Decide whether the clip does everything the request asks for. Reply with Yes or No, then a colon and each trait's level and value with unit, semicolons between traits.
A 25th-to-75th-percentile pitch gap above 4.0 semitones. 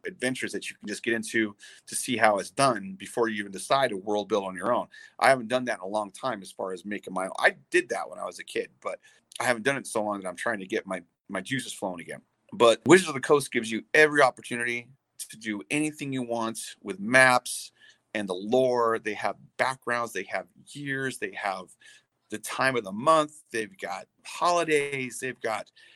Yes: average, 4.6 semitones